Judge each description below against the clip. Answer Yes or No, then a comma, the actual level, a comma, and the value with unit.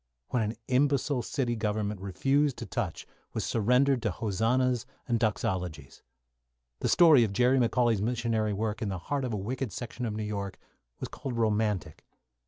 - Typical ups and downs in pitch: Yes, average, 3.2 semitones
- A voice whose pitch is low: Yes, low, 115 Hz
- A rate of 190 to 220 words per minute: No, average, 165 wpm